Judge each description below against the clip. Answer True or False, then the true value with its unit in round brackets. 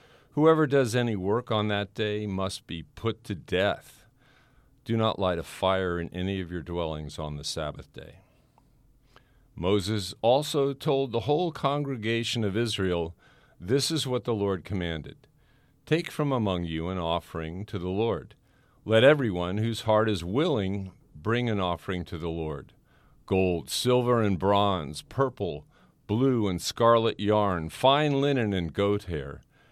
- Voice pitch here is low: True (105 Hz)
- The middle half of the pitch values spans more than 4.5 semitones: True (5.5 semitones)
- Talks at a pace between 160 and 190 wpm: False (150 wpm)